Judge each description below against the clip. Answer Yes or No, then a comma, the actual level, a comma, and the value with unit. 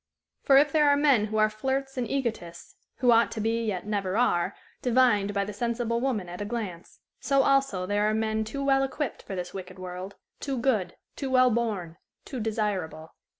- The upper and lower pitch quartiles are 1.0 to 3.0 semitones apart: No, average, 4.7 semitones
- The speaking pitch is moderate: No, high, 220 Hz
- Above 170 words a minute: Yes, average, 195 wpm